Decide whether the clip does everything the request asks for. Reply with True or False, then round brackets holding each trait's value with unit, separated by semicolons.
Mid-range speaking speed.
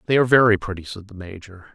False (240 wpm)